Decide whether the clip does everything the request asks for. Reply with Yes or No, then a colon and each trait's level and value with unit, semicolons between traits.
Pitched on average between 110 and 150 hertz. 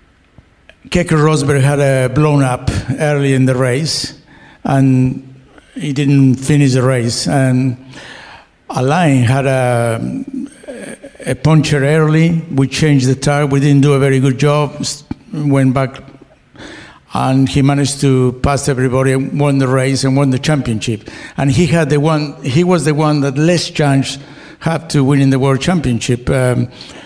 Yes: medium, 140 Hz